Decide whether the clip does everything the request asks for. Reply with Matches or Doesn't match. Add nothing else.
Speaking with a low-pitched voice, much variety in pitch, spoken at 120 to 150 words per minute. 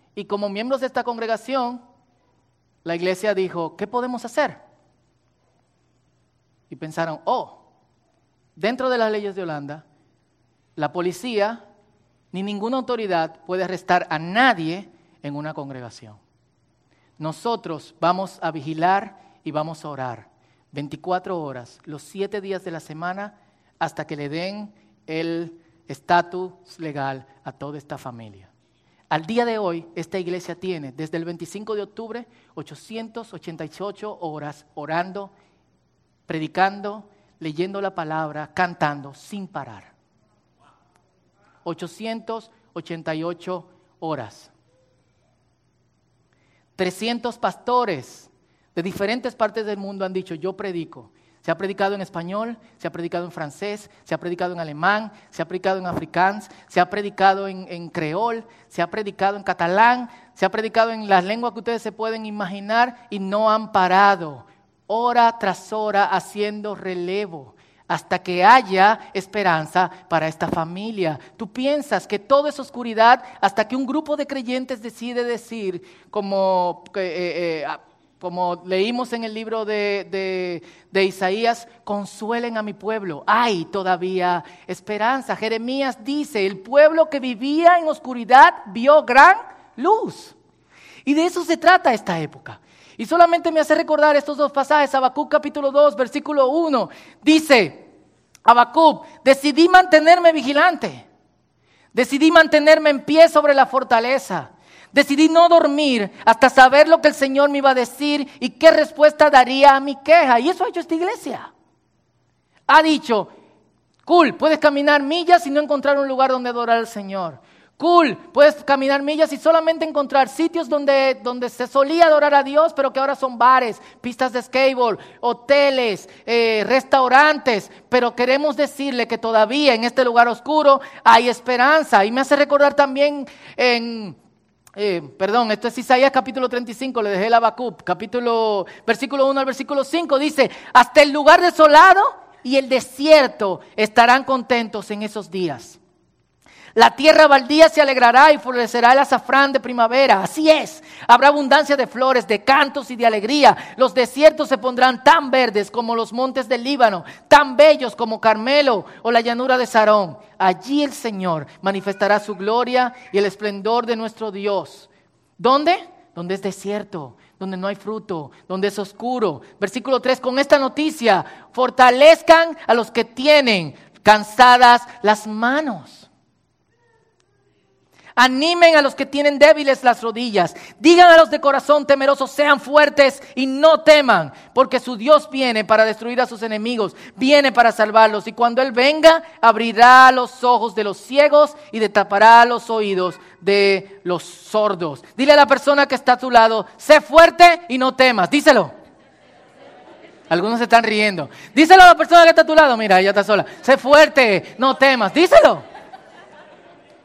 Doesn't match